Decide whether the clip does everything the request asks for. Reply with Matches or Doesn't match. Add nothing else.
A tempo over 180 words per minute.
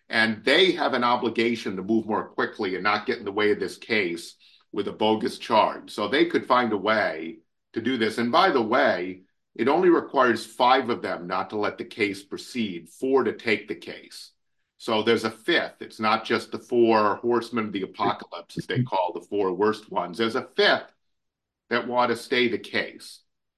Matches